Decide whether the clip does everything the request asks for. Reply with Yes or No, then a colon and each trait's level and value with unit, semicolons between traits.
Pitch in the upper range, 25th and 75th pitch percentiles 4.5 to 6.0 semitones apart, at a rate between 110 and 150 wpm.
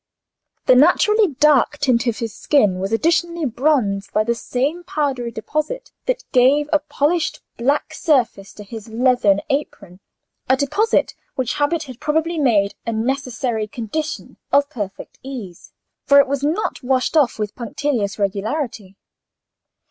Yes: very high, 260 Hz; average, 5.1 semitones; average, 140 wpm